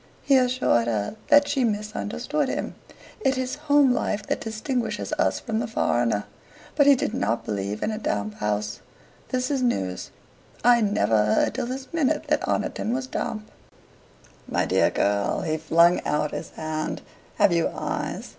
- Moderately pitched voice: No, high, 215 Hz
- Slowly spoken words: No, average, 165 wpm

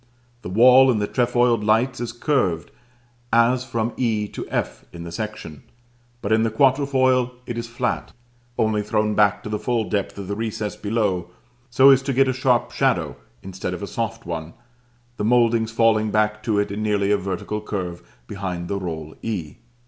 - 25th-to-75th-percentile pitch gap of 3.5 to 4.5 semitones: No, average, 3.1 semitones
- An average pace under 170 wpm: No, average, 185 wpm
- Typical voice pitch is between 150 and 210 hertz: No, low, 110 Hz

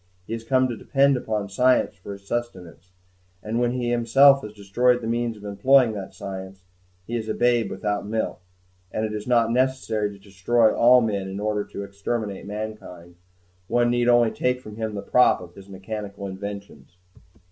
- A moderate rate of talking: Yes, average, 190 wpm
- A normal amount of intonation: Yes, average, 3.2 semitones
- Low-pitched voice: Yes, low, 110 Hz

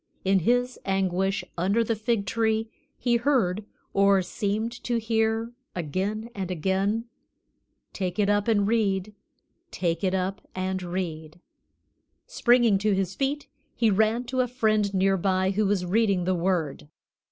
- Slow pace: No, average, 145 wpm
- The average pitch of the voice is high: Yes, high, 200 Hz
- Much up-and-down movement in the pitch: No, average, 3.1 semitones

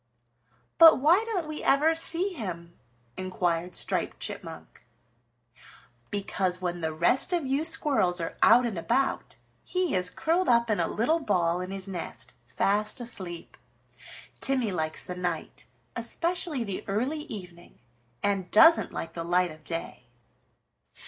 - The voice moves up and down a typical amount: No, wide, 8.8 semitones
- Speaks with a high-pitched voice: Yes, high, 205 Hz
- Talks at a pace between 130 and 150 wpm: Yes, average, 140 wpm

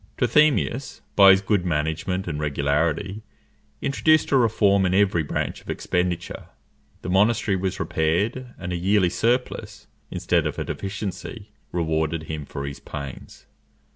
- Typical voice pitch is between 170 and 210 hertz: No, very low, 95 Hz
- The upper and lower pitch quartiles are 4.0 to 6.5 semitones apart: Yes, average, 4.7 semitones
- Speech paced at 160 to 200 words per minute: No, average, 140 wpm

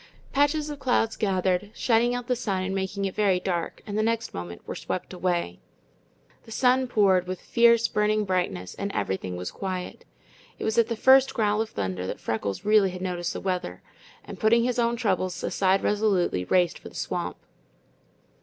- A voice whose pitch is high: Yes, high, 200 Hz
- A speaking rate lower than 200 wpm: Yes, average, 185 wpm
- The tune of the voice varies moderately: Yes, average, 4.1 semitones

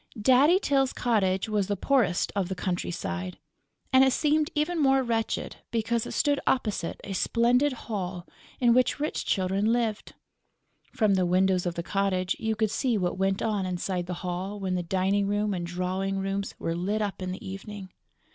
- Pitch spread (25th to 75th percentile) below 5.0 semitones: Yes, average, 4.1 semitones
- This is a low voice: No, high, 200 Hz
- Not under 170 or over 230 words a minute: Yes, average, 180 wpm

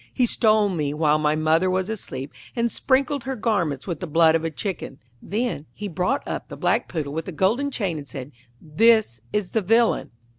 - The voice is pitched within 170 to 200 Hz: Yes, medium, 185 Hz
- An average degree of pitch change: No, wide, 6.4 semitones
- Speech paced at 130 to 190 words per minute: No, average, 200 wpm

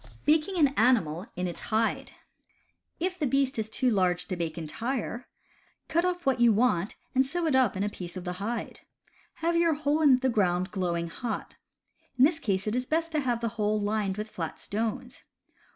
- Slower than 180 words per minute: No, average, 200 wpm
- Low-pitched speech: No, high, 230 Hz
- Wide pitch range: Yes, wide, 6.4 semitones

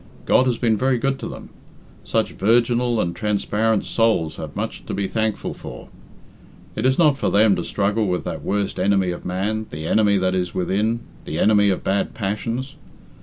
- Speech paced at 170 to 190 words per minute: Yes, average, 185 wpm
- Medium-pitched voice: No, low, 105 Hz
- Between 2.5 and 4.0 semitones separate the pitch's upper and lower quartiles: Yes, average, 3.1 semitones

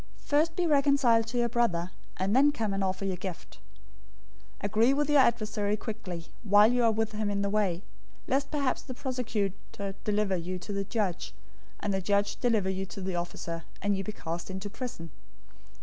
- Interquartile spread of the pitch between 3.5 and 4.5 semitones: Yes, average, 3.9 semitones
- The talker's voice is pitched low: No, high, 205 Hz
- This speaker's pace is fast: No, average, 190 wpm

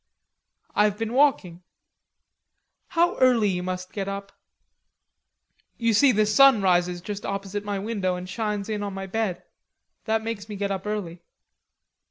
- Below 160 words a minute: Yes, average, 150 wpm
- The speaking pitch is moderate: No, high, 205 Hz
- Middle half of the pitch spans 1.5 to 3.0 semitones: Yes, narrow, 2.6 semitones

